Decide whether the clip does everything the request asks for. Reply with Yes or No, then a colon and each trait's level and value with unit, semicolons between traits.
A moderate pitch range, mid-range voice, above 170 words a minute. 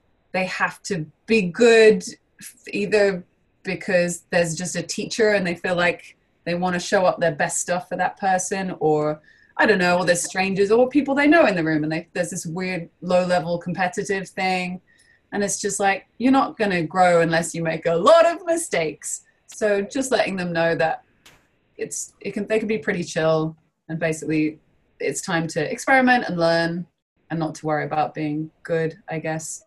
Yes: average, 3.8 semitones; medium, 180 Hz; average, 190 wpm